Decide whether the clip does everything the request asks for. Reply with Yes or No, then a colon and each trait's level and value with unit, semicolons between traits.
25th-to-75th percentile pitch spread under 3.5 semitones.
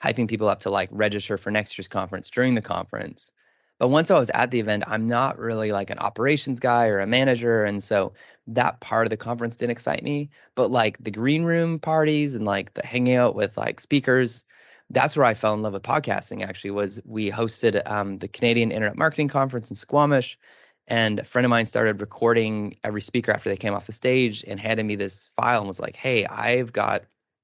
Yes: average, 3.1 semitones